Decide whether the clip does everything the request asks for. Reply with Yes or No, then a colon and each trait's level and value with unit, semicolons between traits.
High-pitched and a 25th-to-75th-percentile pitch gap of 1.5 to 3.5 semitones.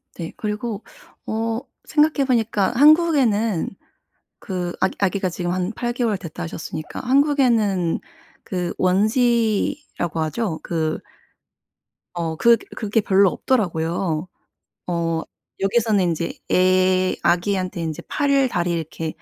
No: high, 195 Hz; average, 5.2 semitones